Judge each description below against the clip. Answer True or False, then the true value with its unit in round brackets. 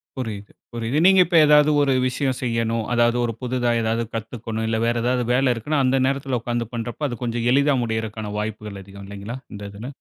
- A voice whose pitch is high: False (120 Hz)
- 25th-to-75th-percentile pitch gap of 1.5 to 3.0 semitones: True (2.7 semitones)